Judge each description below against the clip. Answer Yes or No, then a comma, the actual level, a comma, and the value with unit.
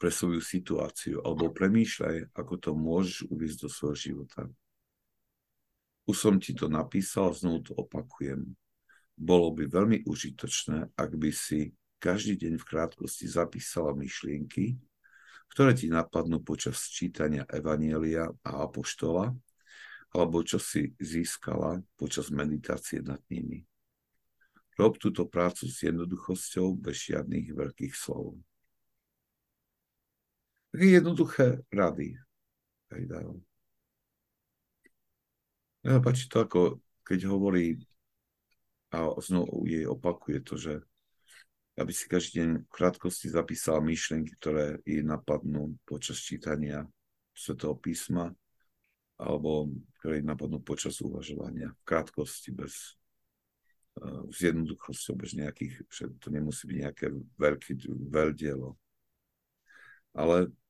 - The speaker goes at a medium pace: No, slow, 105 wpm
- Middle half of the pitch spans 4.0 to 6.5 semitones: No, average, 3.3 semitones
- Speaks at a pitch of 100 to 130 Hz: No, very low, 80 Hz